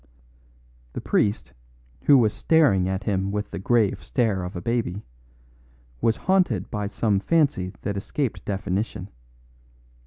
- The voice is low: Yes, low, 105 Hz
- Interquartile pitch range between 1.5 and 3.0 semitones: No, average, 3.9 semitones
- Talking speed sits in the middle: No, slow, 130 wpm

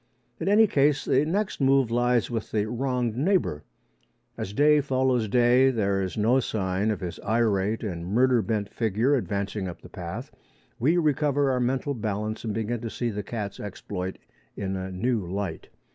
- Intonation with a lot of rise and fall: No, average, 4.6 semitones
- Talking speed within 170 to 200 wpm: Yes, average, 175 wpm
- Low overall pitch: Yes, low, 115 Hz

